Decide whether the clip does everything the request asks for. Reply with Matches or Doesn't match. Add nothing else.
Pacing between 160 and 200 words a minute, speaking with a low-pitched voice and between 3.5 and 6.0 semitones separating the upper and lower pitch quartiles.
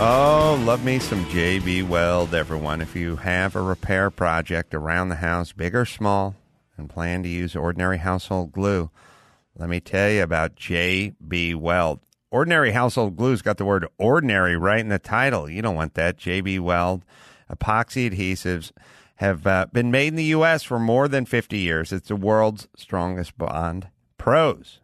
Matches